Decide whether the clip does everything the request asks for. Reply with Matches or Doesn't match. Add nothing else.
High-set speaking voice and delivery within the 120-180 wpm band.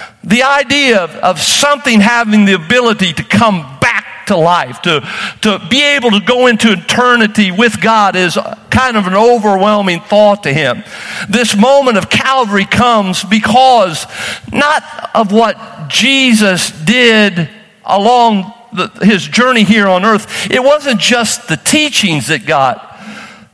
Matches